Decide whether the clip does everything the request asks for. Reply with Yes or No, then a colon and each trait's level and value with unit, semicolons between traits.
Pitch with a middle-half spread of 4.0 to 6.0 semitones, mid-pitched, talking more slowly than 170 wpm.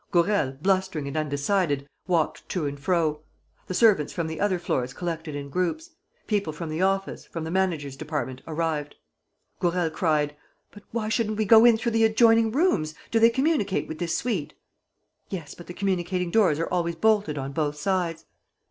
No: average, 5.0 semitones; medium, 175 Hz; average, 175 wpm